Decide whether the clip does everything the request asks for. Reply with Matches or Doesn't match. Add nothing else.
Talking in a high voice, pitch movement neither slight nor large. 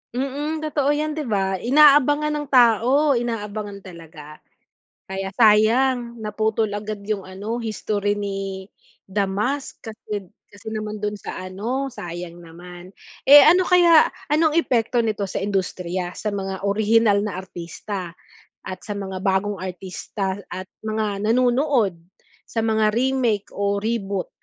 Matches